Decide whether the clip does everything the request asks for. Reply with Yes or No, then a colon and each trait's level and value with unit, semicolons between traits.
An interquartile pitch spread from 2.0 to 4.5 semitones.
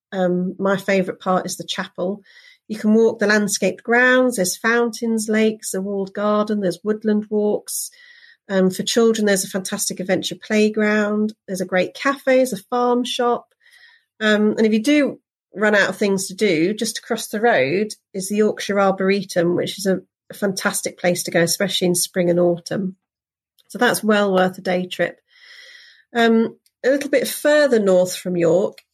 Yes: average, 3.8 semitones